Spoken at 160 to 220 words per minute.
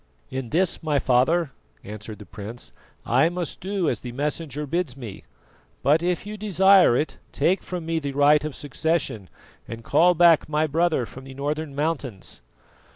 Yes: average, 165 wpm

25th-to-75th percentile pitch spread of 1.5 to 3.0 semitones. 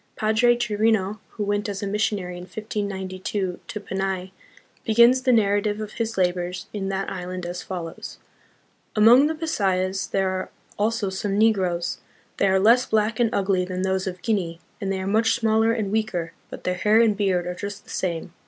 Yes: average, 2.7 semitones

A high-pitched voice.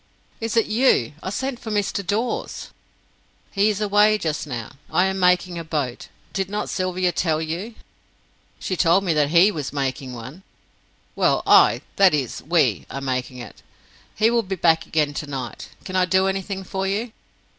No: medium, 180 Hz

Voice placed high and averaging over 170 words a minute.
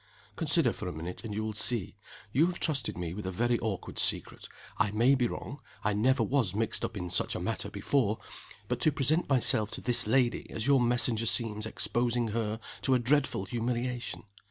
No: low, 120 Hz; average, 200 wpm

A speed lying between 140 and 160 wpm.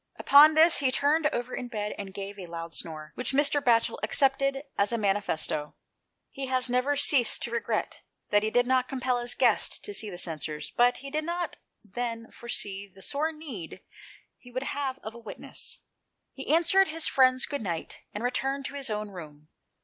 No: average, 190 wpm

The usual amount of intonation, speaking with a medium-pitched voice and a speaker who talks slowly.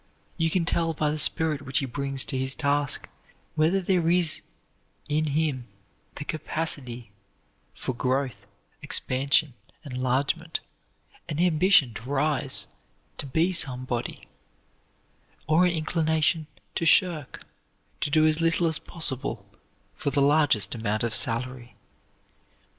Yes: average, 3.8 semitones; medium, 145 Hz; slow, 125 wpm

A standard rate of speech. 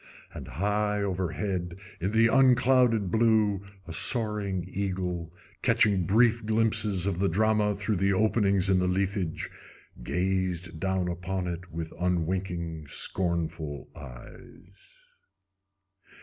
No: slow, 110 wpm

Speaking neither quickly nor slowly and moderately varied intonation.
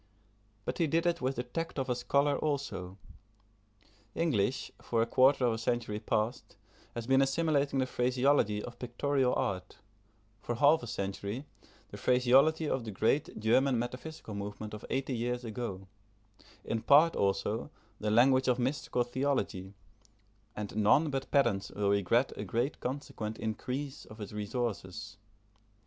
Yes: average, 150 wpm; average, 4.3 semitones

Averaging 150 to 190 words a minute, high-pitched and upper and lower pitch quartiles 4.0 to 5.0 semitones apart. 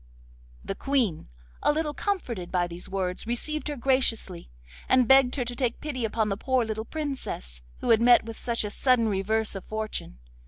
Yes: average, 185 wpm; high, 230 Hz; average, 4.5 semitones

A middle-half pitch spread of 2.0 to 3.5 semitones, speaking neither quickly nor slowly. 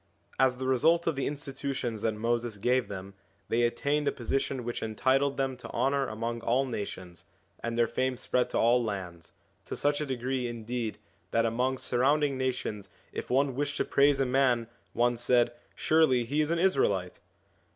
Yes: average, 2.8 semitones; average, 175 wpm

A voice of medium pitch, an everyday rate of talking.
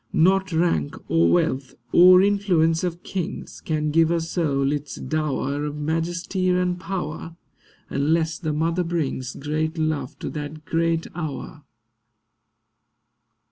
No: medium, 160 Hz; slow, 125 wpm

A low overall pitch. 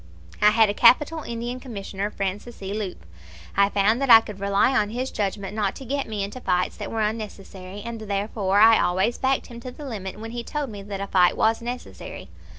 No: high, 215 Hz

